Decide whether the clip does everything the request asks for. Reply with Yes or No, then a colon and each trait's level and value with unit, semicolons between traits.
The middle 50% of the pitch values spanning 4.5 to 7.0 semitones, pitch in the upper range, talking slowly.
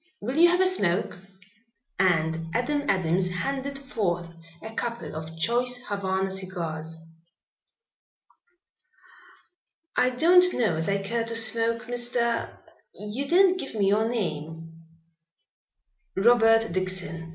Yes: wide, 5.5 semitones; high, 215 Hz; slow, 115 wpm